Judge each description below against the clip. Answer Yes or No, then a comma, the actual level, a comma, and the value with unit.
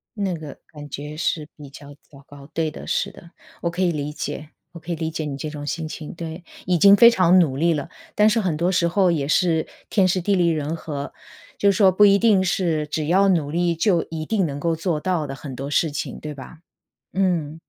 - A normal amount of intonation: Yes, average, 3.5 semitones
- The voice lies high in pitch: No, medium, 165 Hz